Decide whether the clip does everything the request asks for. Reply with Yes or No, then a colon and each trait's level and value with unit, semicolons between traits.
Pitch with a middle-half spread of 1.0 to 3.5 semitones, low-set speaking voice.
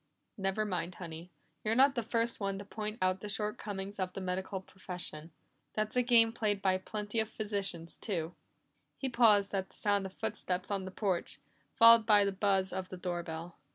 No: narrow, 2.5 semitones; high, 200 Hz